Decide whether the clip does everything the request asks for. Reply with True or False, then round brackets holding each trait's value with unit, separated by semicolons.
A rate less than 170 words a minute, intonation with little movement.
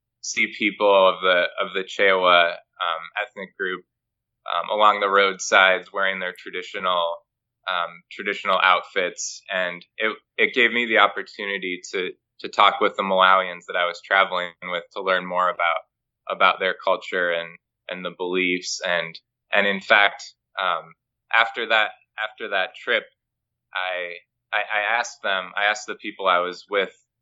True (155 wpm; 2.0 semitones)